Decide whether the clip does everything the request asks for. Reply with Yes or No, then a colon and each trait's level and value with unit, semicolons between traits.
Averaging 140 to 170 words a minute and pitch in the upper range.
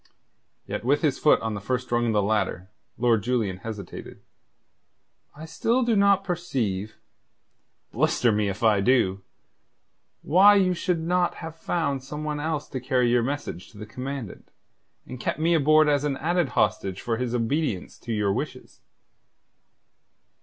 No: average, 160 wpm; low, 130 Hz